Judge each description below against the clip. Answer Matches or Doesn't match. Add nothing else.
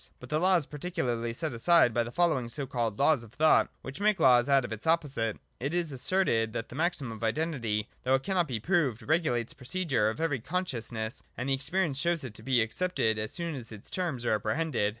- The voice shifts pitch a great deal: Matches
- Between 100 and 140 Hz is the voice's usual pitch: Matches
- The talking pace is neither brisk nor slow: Doesn't match